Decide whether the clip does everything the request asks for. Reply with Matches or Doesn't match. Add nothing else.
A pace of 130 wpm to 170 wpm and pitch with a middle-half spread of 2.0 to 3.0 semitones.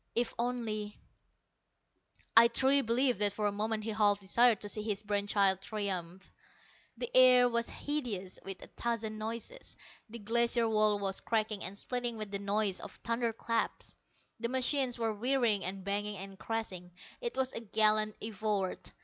Matches